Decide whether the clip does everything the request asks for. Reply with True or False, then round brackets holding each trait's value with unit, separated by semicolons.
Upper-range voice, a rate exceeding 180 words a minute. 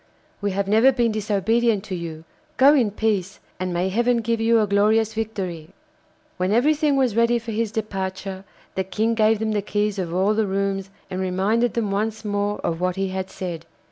True (205 Hz; 195 wpm)